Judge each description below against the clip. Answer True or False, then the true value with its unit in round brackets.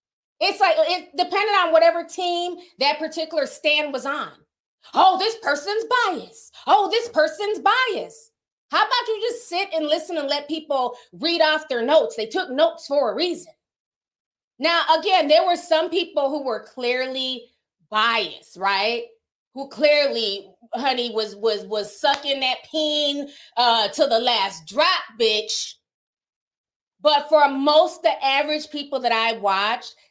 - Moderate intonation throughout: False (5.7 semitones)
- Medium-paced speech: True (150 wpm)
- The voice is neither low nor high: False (300 Hz)